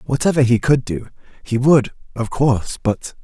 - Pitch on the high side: No, low, 125 Hz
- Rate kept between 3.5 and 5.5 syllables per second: Yes, 5.0 syllables/s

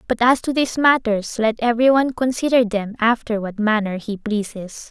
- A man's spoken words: No, female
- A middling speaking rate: Yes, average, 185 wpm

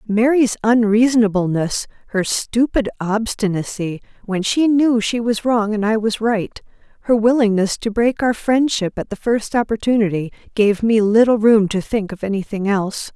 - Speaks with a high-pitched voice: Yes, high, 220 Hz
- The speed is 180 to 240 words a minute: No, average, 155 wpm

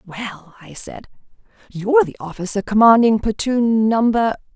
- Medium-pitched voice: No, high, 220 Hz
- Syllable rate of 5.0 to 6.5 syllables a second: No, 4.6 syllables/s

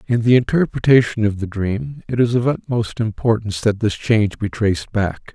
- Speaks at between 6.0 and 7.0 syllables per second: No, 5.3 syllables/s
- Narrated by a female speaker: No, male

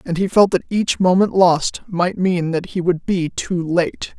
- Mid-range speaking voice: Yes, medium, 180 Hz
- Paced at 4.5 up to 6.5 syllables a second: No, 4.0 syllables/s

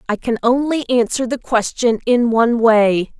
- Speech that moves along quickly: No, average, 170 wpm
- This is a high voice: Yes, high, 235 Hz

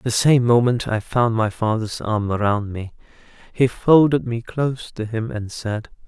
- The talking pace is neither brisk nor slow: Yes, average, 180 wpm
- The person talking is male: Yes, male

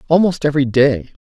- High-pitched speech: No, medium, 140 Hz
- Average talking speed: Yes, average, 145 wpm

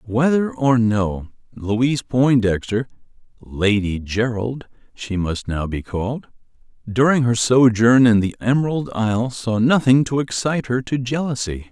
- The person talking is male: Yes, male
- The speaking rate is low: Yes, slow, 130 wpm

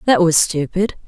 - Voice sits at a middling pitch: Yes, medium, 175 Hz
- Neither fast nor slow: Yes, average, 165 wpm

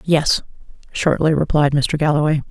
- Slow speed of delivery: Yes, slow, 120 wpm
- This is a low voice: No, medium, 150 Hz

